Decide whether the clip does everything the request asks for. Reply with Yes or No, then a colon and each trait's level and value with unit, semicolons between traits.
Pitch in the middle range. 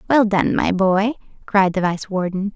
No: high, 195 Hz